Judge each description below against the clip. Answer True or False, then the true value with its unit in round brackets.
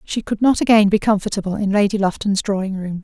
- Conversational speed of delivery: False (215 wpm)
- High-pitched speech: True (205 Hz)